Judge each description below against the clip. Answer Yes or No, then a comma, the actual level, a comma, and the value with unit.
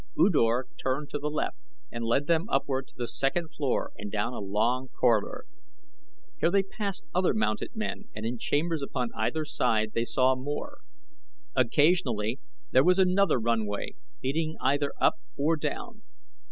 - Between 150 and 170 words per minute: Yes, average, 160 wpm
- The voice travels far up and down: Yes, wide, 5.9 semitones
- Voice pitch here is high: No, low, 135 Hz